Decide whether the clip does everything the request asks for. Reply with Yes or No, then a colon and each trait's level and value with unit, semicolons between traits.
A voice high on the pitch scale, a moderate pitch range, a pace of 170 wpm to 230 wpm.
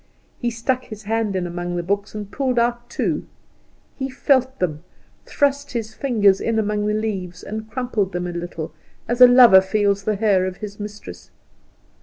Yes: high, 210 Hz; average, 4.1 semitones; average, 180 wpm